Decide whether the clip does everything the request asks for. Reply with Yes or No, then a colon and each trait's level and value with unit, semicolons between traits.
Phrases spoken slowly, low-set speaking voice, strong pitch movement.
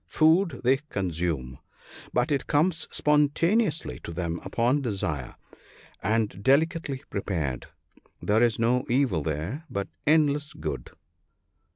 Yes: slow, 110 wpm; low, 125 Hz; wide, 8.8 semitones